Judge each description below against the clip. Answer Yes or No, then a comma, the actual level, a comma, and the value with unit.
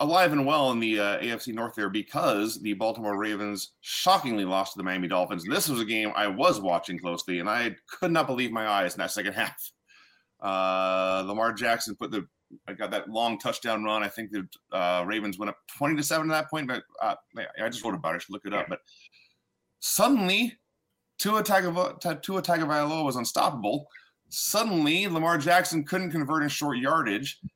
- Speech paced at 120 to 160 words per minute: No, average, 200 wpm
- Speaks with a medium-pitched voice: No, low, 115 Hz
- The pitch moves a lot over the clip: Yes, wide, 7.5 semitones